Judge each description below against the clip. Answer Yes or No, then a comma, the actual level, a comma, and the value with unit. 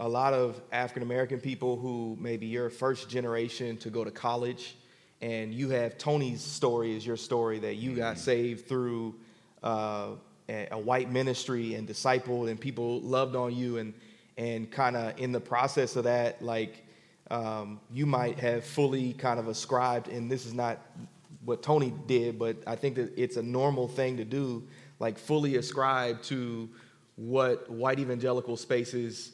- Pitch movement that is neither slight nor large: No, narrow, 1.8 semitones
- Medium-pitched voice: No, low, 120 Hz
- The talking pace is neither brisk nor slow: Yes, average, 165 wpm